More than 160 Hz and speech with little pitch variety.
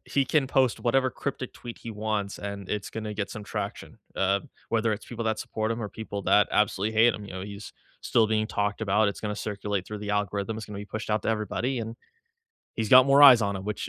No: low, 105 Hz; narrow, 1.9 semitones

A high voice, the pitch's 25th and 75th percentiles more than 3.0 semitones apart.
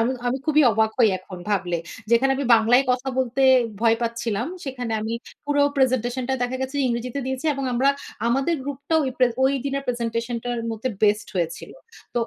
No: high, 245 Hz; average, 2.7 semitones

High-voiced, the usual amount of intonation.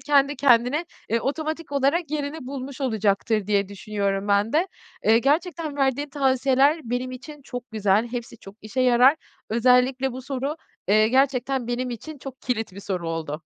Yes: very high, 255 Hz; average, 4.2 semitones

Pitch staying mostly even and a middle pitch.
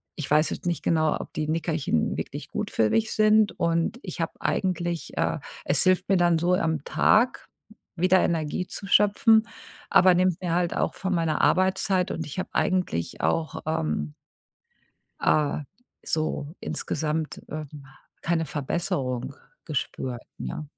No: average, 3.4 semitones; medium, 165 Hz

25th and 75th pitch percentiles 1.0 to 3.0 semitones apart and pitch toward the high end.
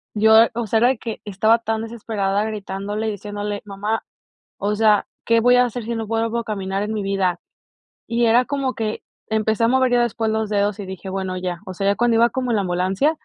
Yes: narrow, 2.5 semitones; high, 220 Hz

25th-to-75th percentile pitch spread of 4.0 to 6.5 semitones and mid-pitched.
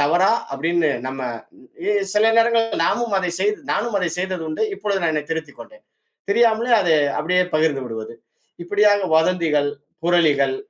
Yes: average, 5.0 semitones; medium, 180 Hz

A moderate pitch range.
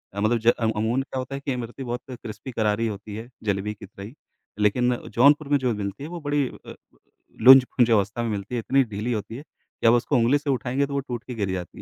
Yes: average, 3.9 semitones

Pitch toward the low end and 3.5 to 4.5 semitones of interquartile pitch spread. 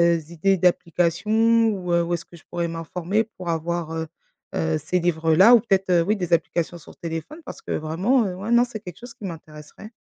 No: medium, 175 Hz; average, 4.0 semitones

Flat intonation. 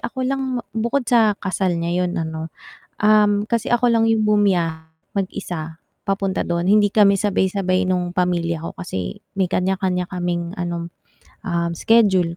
No: average, 3.3 semitones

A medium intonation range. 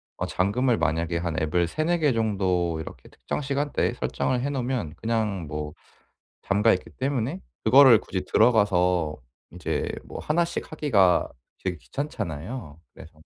No: wide, 7.2 semitones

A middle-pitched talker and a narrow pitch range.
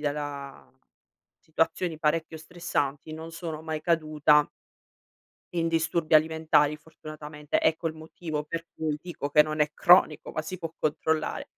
Yes: medium, 155 Hz; narrow, 1.4 semitones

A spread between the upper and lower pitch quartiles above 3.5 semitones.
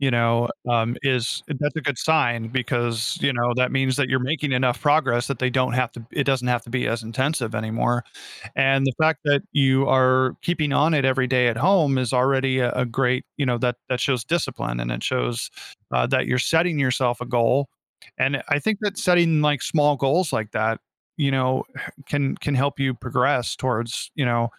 No: average, 2.8 semitones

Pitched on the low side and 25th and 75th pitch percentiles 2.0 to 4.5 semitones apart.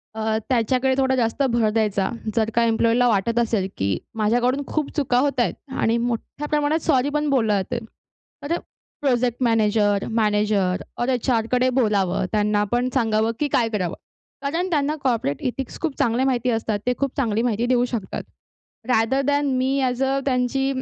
No: high, 240 Hz; average, 3.3 semitones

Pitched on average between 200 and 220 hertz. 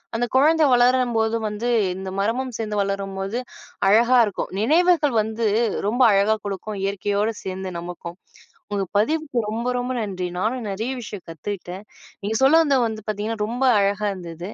Yes: high, 215 Hz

